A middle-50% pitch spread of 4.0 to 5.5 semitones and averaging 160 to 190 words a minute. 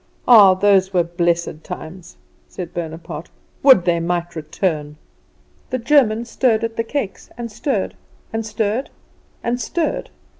No: average, 5.2 semitones; slow, 135 wpm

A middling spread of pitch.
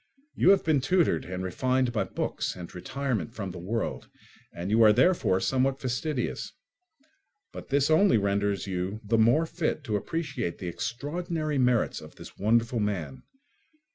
No: wide, 6.1 semitones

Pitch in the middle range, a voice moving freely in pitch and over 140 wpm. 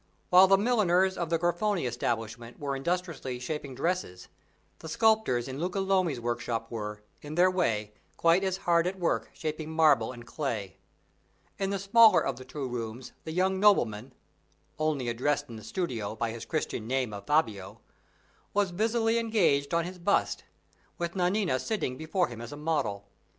Yes: medium, 155 Hz; wide, 7.4 semitones; average, 165 wpm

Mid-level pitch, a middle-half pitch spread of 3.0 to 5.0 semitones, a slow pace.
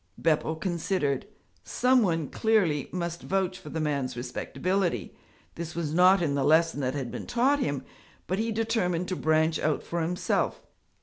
No: medium, 170 Hz; average, 4.0 semitones; average, 165 wpm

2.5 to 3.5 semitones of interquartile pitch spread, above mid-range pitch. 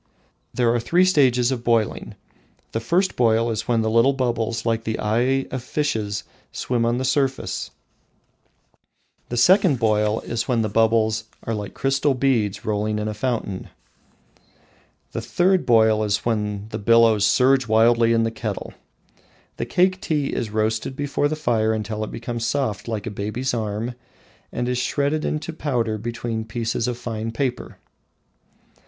No: average, 2.9 semitones; low, 115 Hz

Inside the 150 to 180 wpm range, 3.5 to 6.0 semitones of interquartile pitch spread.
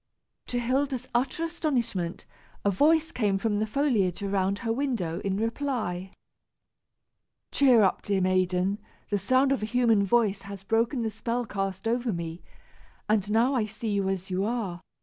Yes: average, 160 wpm; average, 4.2 semitones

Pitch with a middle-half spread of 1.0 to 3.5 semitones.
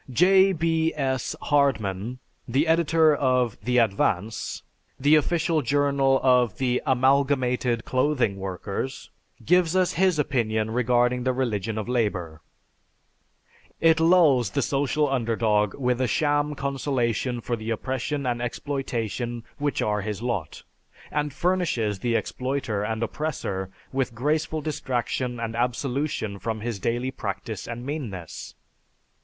No: average, 4.2 semitones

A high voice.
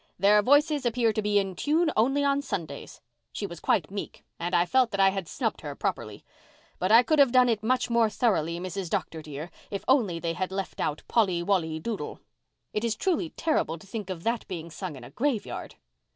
Yes: high, 205 Hz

